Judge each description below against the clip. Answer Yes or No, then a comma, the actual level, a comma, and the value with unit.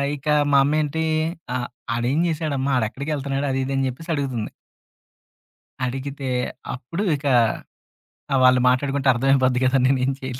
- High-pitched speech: No, low, 135 Hz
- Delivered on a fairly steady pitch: Yes, narrow, 1.9 semitones